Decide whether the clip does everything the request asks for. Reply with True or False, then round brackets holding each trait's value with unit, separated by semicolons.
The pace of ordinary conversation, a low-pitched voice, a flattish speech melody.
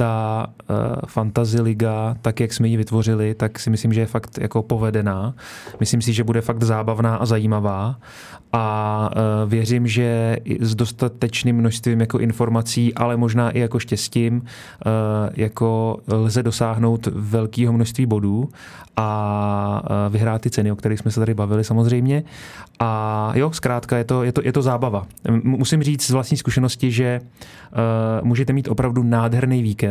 True (150 wpm; 115 Hz; 1.8 semitones)